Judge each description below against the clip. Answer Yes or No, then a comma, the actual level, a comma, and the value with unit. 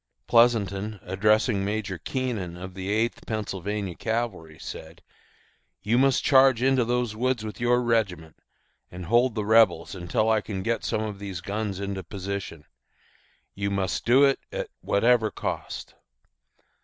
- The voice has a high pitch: No, low, 105 Hz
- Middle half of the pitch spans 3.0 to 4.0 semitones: Yes, average, 3.7 semitones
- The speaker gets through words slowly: No, average, 145 wpm